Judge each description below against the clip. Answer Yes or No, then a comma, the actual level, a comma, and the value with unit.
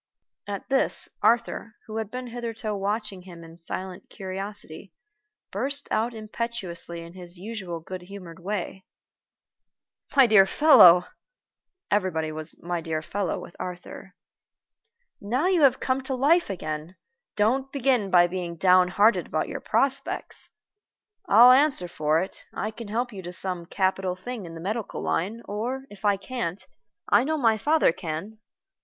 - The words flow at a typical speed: Yes, average, 150 wpm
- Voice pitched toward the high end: Yes, high, 200 Hz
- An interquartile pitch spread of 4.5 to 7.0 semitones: Yes, average, 4.8 semitones